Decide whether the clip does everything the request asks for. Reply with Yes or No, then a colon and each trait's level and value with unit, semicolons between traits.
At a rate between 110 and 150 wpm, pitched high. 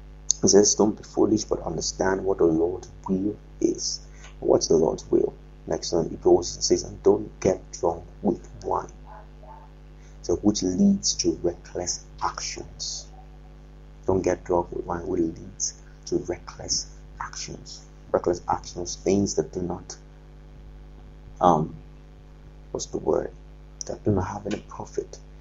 Yes: average, 140 wpm; very high, 340 Hz